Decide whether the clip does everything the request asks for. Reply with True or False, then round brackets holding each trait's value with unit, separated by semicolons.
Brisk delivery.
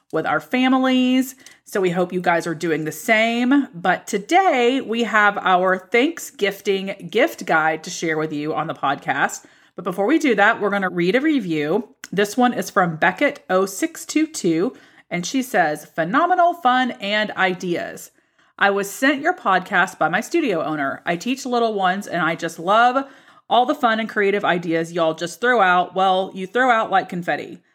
False (180 wpm)